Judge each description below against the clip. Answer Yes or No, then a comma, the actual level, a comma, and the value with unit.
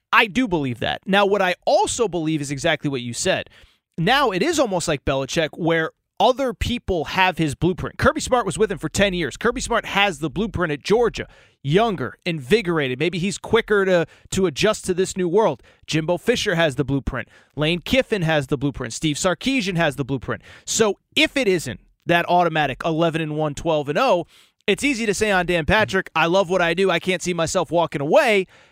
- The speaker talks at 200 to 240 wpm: Yes, fast, 205 wpm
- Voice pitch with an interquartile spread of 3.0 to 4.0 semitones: No, average, 4.6 semitones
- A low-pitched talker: No, medium, 175 Hz